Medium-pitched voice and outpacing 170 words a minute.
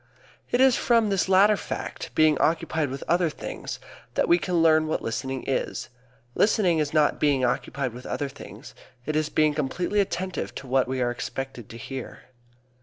Yes: medium, 155 Hz; average, 180 wpm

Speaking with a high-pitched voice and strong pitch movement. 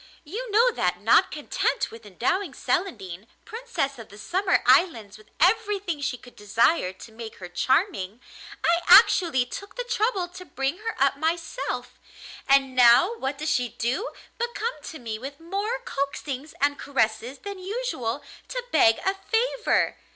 Yes: very high, 300 Hz; wide, 8.6 semitones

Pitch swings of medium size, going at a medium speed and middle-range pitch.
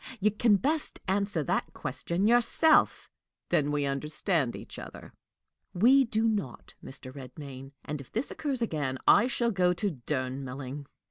No: wide, 8.3 semitones; average, 145 wpm; medium, 170 Hz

